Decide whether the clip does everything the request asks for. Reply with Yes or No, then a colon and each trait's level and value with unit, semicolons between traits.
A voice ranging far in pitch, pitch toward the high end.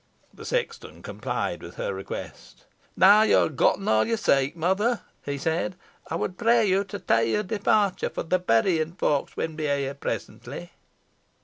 No: wide, 6.7 semitones; medium, 180 Hz